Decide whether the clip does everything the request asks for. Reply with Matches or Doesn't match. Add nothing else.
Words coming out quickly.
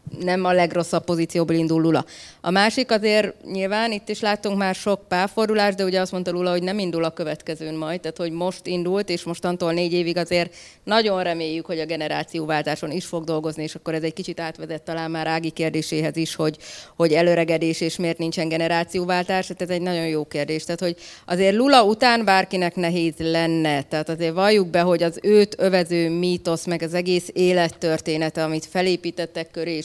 Matches